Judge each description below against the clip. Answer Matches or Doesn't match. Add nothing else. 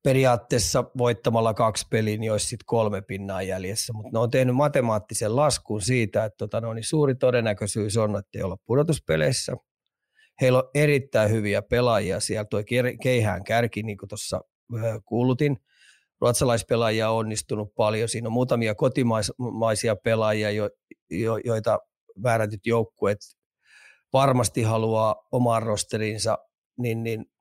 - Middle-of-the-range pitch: Doesn't match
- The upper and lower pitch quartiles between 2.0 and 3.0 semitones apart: Matches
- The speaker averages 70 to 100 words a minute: Doesn't match